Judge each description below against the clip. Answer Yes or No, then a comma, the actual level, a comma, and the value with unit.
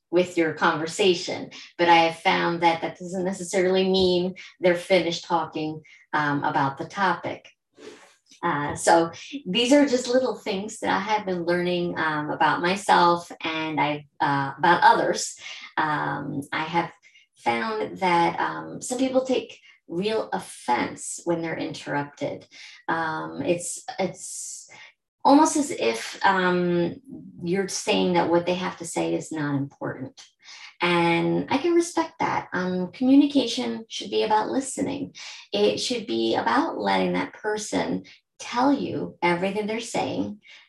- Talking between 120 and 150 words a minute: Yes, average, 140 wpm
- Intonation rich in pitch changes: No, average, 4.7 semitones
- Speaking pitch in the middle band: Yes, medium, 180 Hz